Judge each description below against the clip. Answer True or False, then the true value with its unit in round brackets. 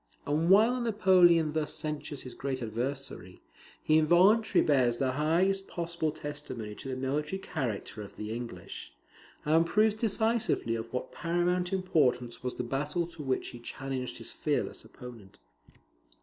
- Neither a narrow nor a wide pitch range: False (5.8 semitones)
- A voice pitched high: False (150 Hz)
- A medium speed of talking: True (145 wpm)